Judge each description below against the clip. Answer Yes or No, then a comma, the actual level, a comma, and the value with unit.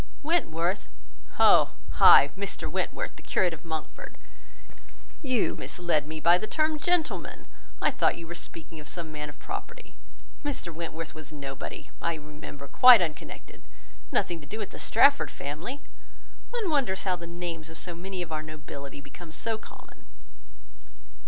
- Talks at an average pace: Yes, average, 150 wpm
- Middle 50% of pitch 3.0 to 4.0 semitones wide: No, average, 4.8 semitones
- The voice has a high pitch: No, medium, 170 Hz